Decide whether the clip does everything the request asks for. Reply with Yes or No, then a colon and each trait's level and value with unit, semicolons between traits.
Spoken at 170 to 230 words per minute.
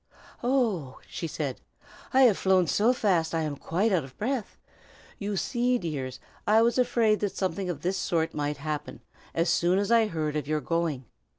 Yes: average, 185 wpm